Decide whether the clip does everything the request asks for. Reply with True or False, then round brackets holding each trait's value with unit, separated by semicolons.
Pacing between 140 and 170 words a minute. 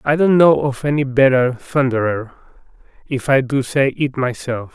True (165 wpm)